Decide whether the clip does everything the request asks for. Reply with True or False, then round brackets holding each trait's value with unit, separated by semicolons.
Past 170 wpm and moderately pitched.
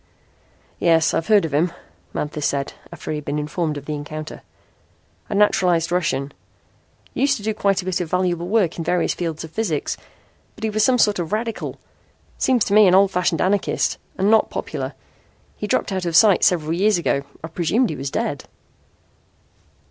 True (185 wpm; 180 Hz)